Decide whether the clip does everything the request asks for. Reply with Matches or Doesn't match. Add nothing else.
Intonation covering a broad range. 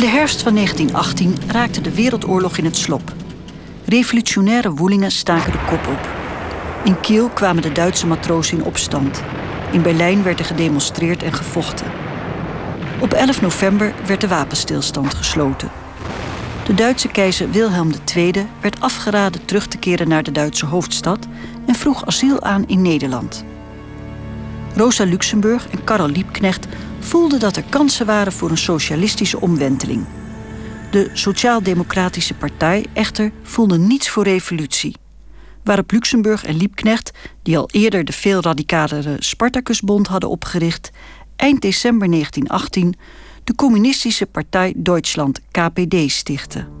Doesn't match